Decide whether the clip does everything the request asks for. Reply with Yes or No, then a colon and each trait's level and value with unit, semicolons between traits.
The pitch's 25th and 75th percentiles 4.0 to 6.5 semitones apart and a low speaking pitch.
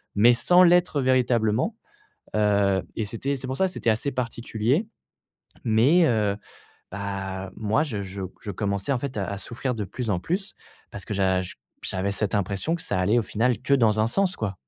Yes: average, 4.6 semitones; low, 110 Hz